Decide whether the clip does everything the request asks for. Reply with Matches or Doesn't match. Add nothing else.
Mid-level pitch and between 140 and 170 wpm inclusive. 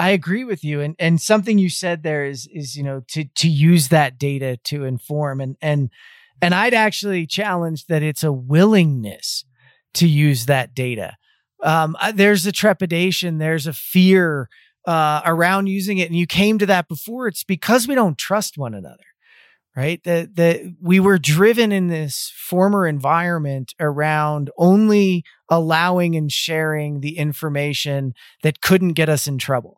Matches